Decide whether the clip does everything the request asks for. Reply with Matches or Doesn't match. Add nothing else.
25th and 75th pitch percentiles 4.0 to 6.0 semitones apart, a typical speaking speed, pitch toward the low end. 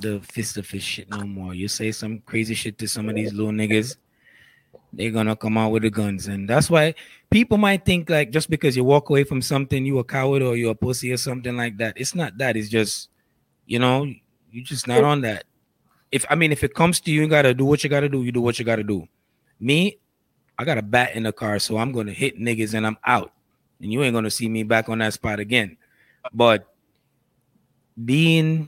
Doesn't match